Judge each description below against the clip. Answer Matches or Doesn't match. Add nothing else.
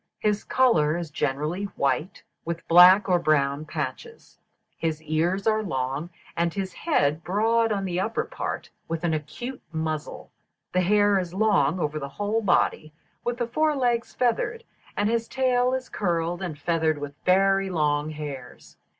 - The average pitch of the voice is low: Doesn't match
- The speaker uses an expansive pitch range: Matches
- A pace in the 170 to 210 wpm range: Doesn't match